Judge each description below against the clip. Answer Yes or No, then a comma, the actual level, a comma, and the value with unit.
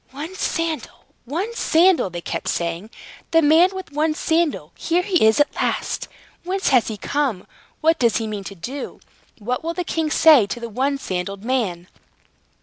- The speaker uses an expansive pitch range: Yes, wide, 7.2 semitones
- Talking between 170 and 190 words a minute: Yes, average, 175 wpm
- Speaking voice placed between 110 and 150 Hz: No, very high, 285 Hz